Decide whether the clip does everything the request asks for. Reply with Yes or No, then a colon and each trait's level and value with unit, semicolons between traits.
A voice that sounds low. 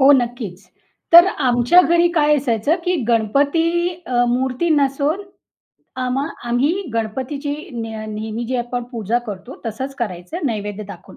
No: very high, 250 Hz